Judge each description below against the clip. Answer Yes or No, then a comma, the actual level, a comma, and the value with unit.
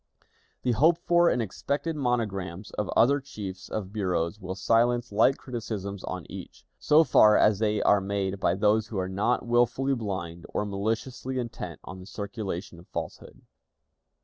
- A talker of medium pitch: No, low, 105 Hz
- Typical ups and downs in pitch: Yes, average, 4.1 semitones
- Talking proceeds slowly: No, average, 160 wpm